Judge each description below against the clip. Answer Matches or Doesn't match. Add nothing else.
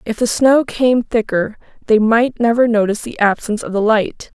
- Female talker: Matches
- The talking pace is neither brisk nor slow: Matches